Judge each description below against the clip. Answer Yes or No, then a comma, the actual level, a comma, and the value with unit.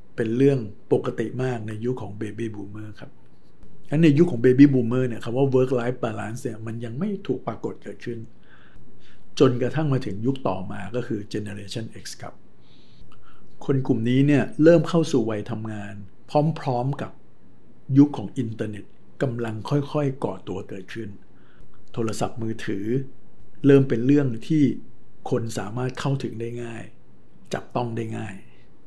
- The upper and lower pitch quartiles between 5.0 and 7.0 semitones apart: No, average, 3.8 semitones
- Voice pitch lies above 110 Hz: Yes, low, 120 Hz